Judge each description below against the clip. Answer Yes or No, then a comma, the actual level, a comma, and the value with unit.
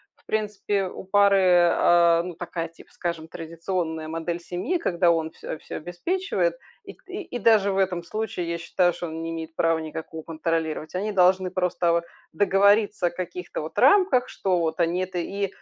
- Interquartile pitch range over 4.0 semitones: No, average, 3.1 semitones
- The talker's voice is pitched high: No, medium, 175 Hz